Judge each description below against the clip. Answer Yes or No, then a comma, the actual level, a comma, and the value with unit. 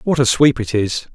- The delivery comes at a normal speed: No, fast, 260 wpm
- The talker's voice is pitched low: Yes, low, 120 Hz